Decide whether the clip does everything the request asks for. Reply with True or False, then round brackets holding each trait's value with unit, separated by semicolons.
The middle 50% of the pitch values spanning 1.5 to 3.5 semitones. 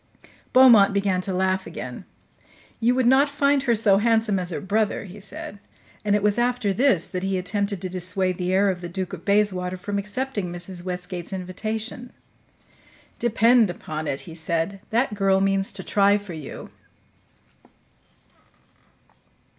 True (3.1 semitones)